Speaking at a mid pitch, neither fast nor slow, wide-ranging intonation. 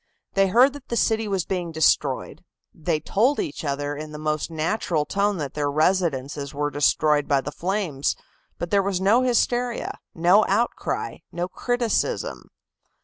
Yes: medium, 175 Hz; average, 155 wpm; wide, 5.7 semitones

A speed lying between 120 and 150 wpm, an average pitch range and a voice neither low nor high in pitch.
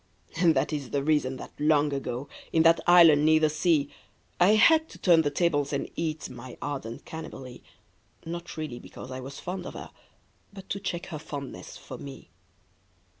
No: average, 185 wpm; average, 3.4 semitones; medium, 155 Hz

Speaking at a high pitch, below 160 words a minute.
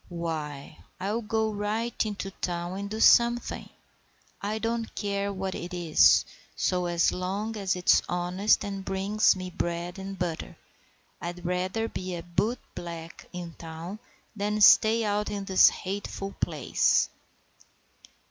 Yes: high, 195 Hz; slow, 135 wpm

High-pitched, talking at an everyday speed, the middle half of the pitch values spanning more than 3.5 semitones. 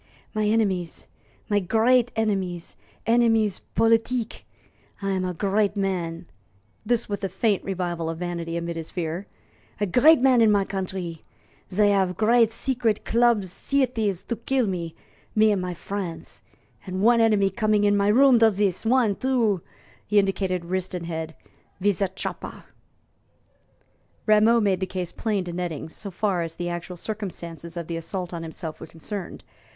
Yes: high, 195 Hz; average, 160 wpm; average, 4.0 semitones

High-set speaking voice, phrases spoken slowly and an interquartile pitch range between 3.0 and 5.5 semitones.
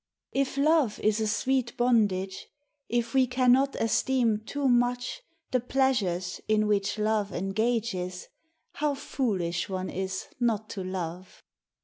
Yes: high, 220 Hz; slow, 125 wpm; average, 4.7 semitones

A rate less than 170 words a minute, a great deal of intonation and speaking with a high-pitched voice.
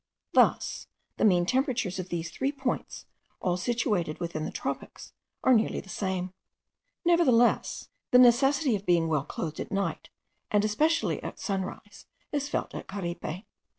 Yes: average, 145 wpm; wide, 6.3 semitones; high, 205 Hz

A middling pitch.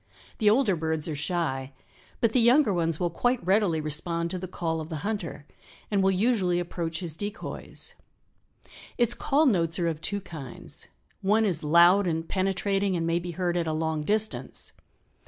Yes: medium, 175 Hz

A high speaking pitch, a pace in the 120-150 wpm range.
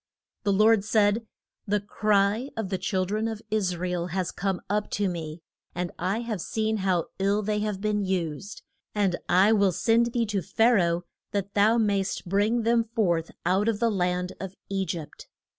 No: high, 200 Hz; average, 195 wpm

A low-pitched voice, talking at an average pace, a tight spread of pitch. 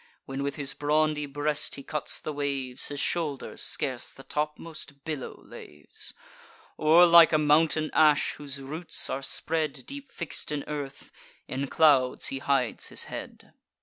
No: medium, 150 Hz; average, 150 wpm; narrow, 2.0 semitones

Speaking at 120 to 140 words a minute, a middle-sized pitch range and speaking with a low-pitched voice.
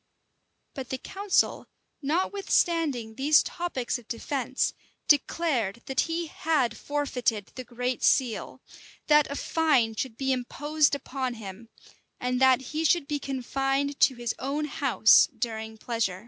No: slow, 135 wpm; average, 3.8 semitones; very high, 265 Hz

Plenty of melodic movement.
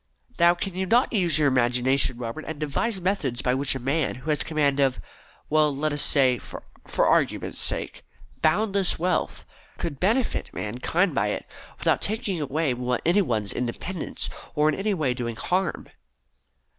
Yes: wide, 5.7 semitones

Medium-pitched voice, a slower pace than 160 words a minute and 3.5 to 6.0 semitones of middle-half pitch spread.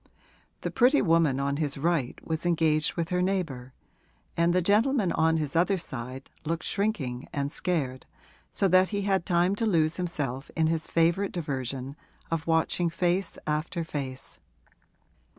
Yes: medium, 165 Hz; average, 150 wpm; average, 4.0 semitones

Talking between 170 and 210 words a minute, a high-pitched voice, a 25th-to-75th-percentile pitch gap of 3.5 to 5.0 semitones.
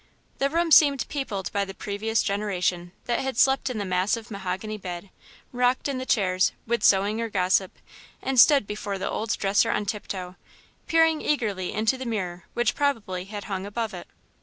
Yes: average, 180 wpm; high, 210 Hz; average, 4.5 semitones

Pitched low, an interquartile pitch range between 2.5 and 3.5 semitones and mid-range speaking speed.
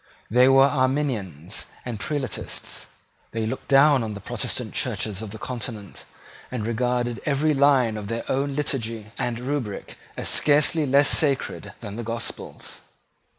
No: low, 125 Hz; average, 3.9 semitones; average, 145 wpm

